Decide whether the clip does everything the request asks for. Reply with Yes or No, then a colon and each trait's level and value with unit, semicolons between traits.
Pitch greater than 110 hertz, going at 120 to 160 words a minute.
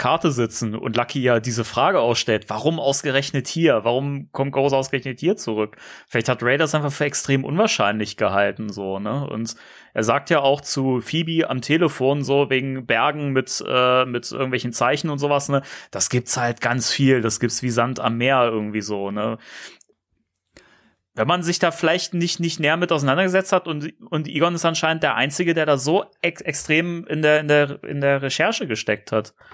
No: low, 135 Hz; fast, 190 wpm